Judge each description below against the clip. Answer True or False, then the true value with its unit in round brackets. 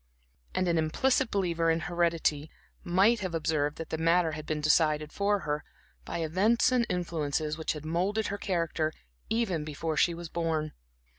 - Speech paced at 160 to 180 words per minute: True (165 wpm)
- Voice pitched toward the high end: False (165 Hz)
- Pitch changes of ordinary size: True (3.0 semitones)